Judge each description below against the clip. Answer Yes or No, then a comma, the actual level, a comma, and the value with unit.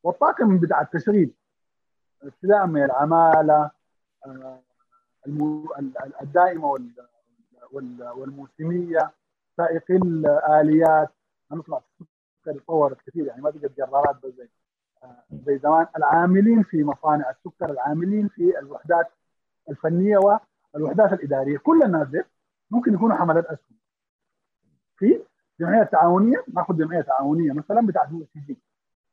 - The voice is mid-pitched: Yes, medium, 160 Hz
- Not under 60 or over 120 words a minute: Yes, average, 105 wpm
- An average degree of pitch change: Yes, average, 4.6 semitones